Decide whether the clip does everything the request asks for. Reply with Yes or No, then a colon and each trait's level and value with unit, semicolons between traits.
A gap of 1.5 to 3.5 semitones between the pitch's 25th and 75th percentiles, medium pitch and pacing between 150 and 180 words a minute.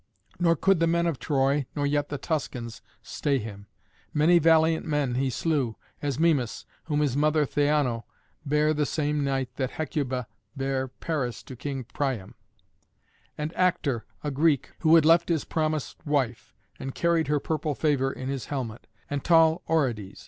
Yes: average, 3.1 semitones; medium, 145 Hz; average, 165 wpm